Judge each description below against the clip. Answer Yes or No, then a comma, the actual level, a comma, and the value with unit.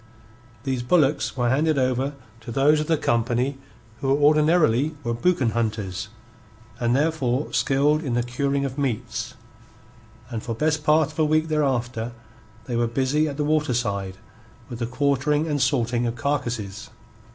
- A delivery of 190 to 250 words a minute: No, average, 150 wpm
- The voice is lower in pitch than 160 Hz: Yes, low, 135 Hz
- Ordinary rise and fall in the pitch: Yes, average, 4.0 semitones